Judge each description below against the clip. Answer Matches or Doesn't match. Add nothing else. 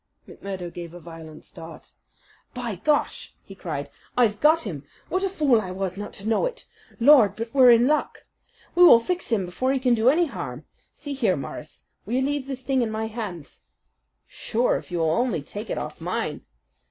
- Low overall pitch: Doesn't match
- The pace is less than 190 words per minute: Doesn't match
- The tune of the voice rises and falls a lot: Matches